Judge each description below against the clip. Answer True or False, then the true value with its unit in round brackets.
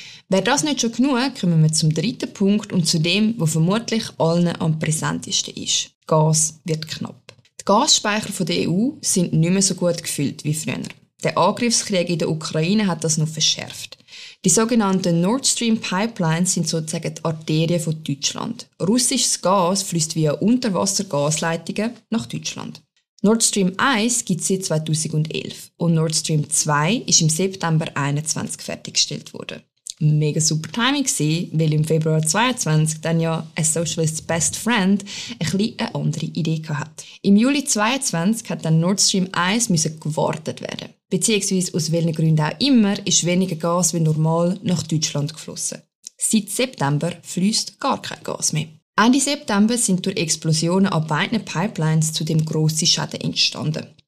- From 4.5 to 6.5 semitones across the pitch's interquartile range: True (4.8 semitones)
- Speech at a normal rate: True (160 wpm)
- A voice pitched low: False (175 Hz)